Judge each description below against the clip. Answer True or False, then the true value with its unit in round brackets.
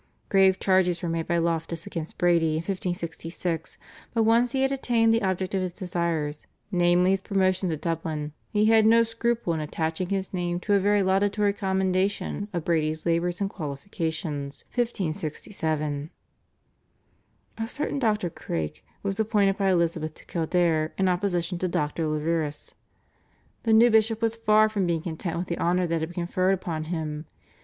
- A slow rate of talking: False (165 wpm)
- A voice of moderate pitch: True (180 Hz)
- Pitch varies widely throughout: False (3.7 semitones)